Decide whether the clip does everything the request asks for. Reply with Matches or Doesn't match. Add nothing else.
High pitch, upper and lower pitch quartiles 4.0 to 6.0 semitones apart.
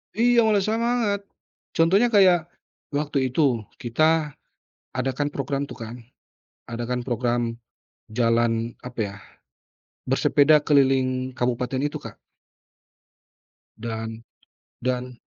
Doesn't match